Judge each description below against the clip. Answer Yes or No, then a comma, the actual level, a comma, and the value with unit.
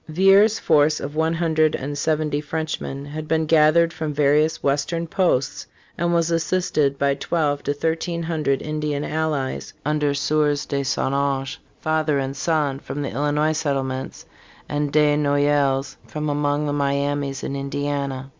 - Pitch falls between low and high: Yes, medium, 145 Hz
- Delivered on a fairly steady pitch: Yes, narrow, 2.0 semitones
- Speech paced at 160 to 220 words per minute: No, average, 150 wpm